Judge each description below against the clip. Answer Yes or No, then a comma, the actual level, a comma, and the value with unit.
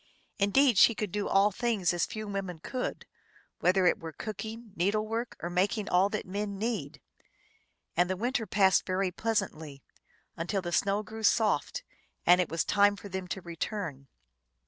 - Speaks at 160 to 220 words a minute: Yes, average, 170 wpm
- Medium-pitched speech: No, high, 200 Hz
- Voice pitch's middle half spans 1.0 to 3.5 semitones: Yes, average, 3.2 semitones